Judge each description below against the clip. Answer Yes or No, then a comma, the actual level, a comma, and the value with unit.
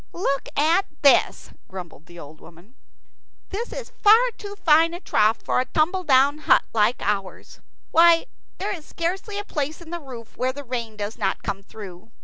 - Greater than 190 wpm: No, average, 175 wpm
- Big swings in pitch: Yes, wide, 8.5 semitones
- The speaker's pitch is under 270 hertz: No, very high, 280 Hz